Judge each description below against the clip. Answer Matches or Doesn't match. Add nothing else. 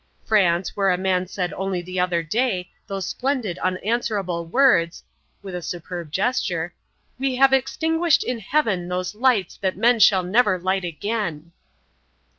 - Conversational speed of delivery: Matches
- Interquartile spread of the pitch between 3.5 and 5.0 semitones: Matches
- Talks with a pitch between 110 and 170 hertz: Doesn't match